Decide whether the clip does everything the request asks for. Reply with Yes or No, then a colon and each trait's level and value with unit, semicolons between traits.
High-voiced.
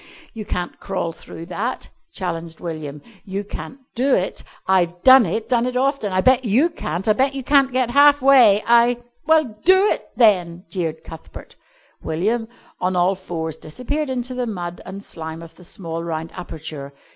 Yes: high, 200 Hz